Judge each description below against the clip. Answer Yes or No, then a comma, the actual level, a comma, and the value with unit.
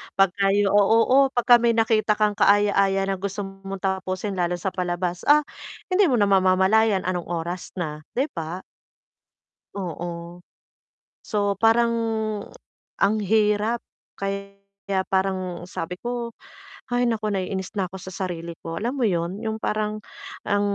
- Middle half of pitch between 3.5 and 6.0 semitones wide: No, narrow, 2.6 semitones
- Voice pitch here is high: Yes, high, 195 Hz